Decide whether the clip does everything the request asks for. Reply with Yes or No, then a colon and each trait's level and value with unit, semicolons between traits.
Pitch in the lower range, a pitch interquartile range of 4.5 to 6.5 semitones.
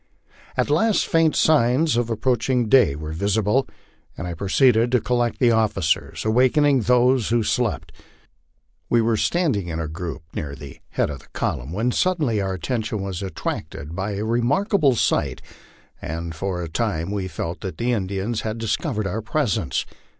Yes: low, 110 Hz; average, 5.2 semitones